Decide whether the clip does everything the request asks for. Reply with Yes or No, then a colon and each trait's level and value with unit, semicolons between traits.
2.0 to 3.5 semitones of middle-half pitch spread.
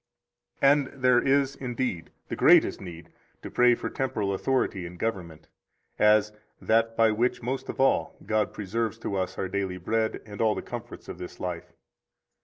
No: average, 4.4 semitones